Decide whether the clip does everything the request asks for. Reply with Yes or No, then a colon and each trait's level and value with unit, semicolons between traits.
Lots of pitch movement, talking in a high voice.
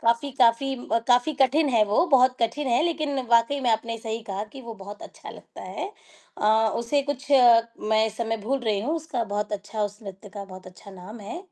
No: average, 4.1 semitones; high, 230 Hz